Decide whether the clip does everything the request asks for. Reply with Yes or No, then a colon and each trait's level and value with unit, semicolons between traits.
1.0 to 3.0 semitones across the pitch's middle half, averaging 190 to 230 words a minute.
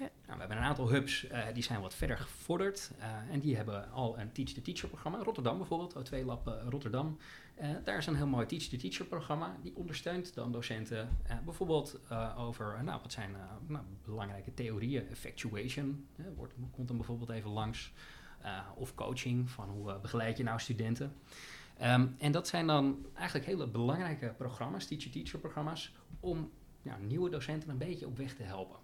No: average, 4.6 semitones; average, 195 wpm